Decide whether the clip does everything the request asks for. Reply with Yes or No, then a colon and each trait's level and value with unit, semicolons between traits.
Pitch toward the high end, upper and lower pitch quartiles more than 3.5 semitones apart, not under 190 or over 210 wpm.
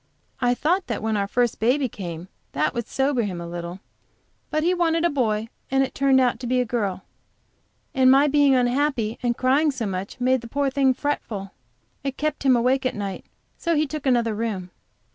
Yes: very high, 250 Hz; average, 4.2 semitones; average, 200 wpm